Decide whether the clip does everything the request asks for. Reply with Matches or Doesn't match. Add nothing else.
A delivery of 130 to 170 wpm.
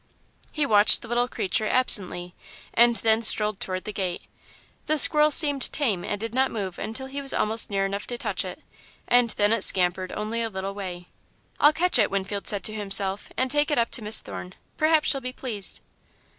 Doesn't match